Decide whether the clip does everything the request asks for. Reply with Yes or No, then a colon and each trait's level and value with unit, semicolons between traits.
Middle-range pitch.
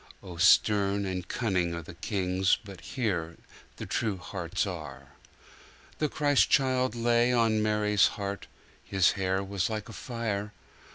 No: low, 100 Hz